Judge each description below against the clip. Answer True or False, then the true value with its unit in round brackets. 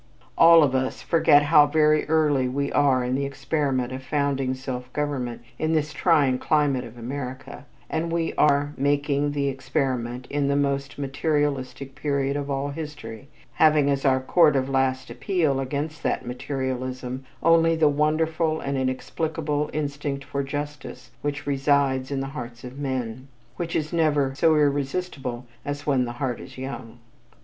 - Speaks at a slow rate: False (160 wpm)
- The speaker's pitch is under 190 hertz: True (140 Hz)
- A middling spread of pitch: False (2.2 semitones)